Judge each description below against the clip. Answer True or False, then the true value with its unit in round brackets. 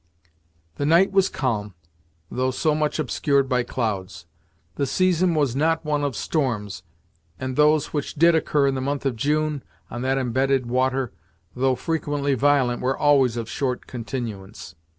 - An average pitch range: True (3.2 semitones)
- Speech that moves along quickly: False (155 wpm)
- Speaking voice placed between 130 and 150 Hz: True (135 Hz)